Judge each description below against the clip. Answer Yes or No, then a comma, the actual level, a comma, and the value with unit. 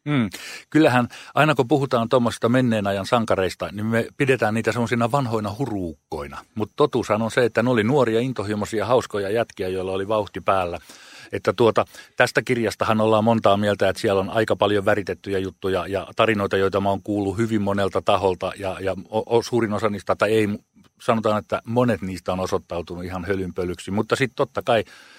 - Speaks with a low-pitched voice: Yes, low, 105 Hz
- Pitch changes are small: No, average, 3.2 semitones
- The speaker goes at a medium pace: No, fast, 175 wpm